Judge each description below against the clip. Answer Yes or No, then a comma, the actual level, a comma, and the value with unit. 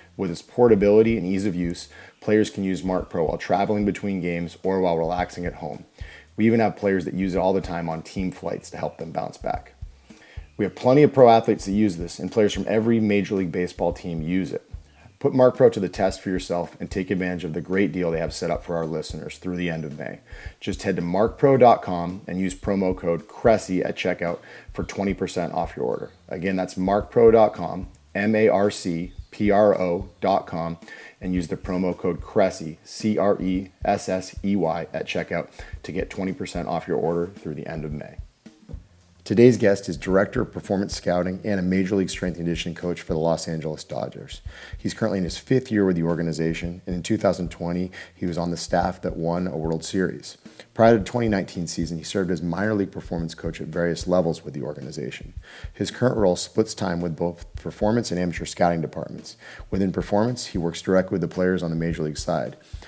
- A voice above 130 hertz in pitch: No, very low, 90 Hz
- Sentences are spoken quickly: Yes, fast, 210 wpm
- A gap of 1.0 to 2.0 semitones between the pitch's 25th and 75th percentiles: No, average, 2.7 semitones